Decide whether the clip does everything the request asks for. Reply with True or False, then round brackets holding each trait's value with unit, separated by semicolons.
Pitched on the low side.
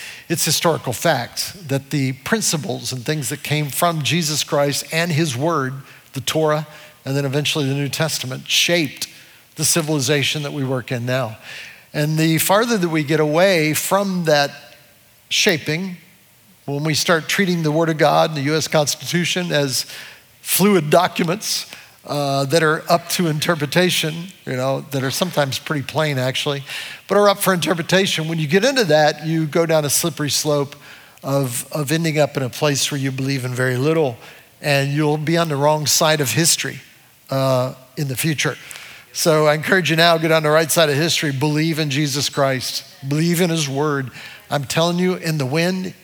False (150 Hz)